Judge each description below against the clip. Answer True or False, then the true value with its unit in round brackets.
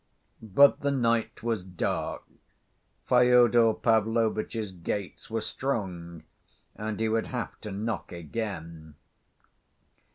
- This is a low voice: True (110 Hz)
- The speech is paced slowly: True (100 wpm)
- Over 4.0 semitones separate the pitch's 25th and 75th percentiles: False (3.7 semitones)